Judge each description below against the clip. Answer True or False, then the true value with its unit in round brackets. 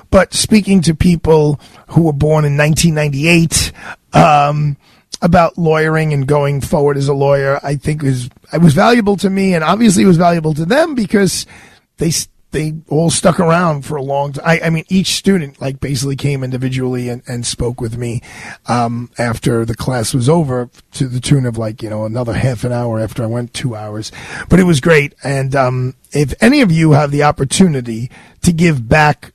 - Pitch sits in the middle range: True (145 Hz)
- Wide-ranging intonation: False (4.6 semitones)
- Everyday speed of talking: True (195 wpm)